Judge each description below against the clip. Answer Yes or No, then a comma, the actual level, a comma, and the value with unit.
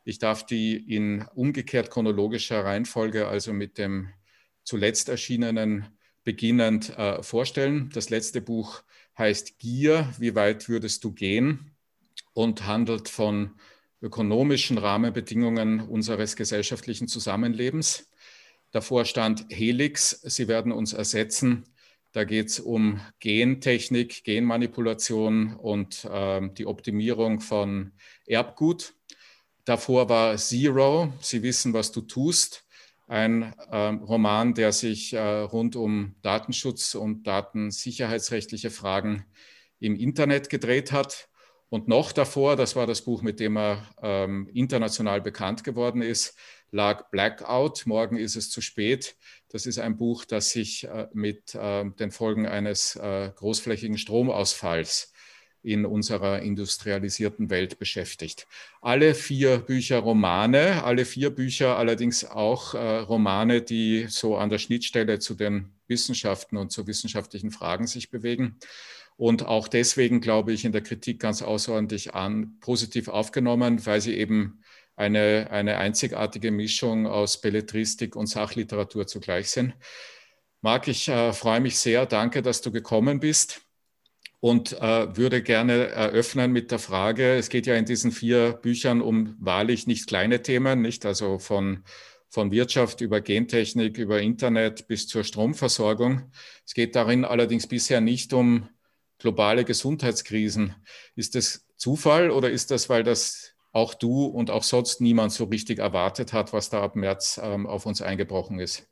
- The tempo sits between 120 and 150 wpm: Yes, slow, 135 wpm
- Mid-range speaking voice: No, low, 115 Hz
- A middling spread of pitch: No, narrow, 2.3 semitones